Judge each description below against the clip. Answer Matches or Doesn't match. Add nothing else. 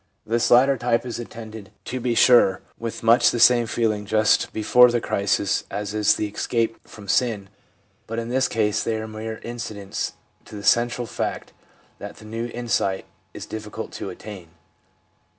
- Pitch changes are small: Matches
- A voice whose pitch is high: Doesn't match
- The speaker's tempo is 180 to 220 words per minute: Doesn't match